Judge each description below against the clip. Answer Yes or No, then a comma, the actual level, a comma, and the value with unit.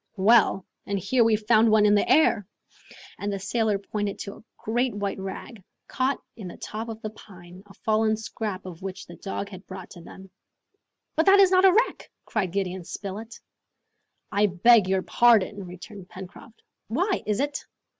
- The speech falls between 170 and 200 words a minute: Yes, average, 180 wpm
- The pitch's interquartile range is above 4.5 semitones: No, average, 3.2 semitones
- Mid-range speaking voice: No, high, 210 Hz